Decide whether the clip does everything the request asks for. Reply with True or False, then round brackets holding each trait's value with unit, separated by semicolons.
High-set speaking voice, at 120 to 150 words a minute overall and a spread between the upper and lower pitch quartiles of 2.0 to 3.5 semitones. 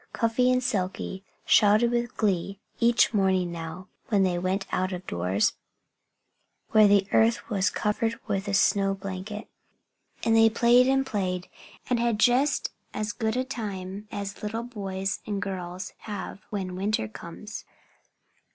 True (205 Hz; 145 wpm; 3.2 semitones)